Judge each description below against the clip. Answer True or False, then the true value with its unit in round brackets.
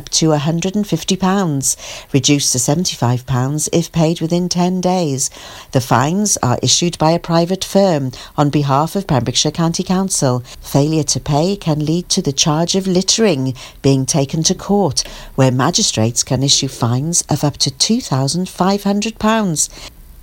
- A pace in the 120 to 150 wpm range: True (140 wpm)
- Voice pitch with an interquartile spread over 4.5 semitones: True (5.2 semitones)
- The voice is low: False (155 Hz)